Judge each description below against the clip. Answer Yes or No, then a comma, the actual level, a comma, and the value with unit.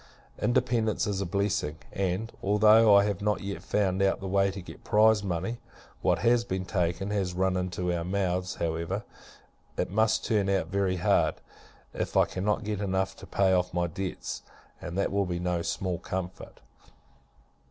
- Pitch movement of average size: No, narrow, 2.3 semitones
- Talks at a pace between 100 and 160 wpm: No, average, 175 wpm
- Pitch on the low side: Yes, very low, 95 Hz